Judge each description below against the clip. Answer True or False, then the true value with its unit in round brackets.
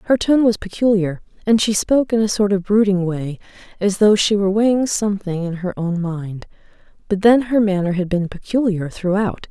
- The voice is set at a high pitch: True (200 Hz)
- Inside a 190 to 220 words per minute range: True (195 wpm)